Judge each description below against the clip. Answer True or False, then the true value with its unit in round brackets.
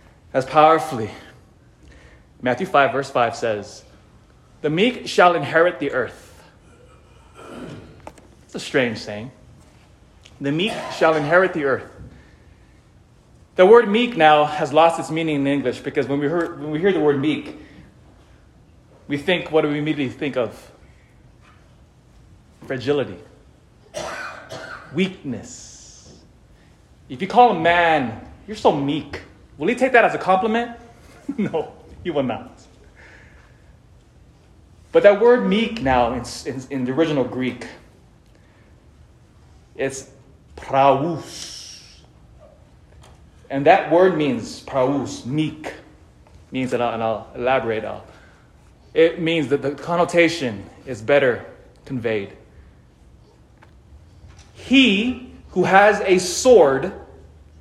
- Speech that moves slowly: True (110 wpm)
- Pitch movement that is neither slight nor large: False (6.3 semitones)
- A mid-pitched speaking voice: True (145 Hz)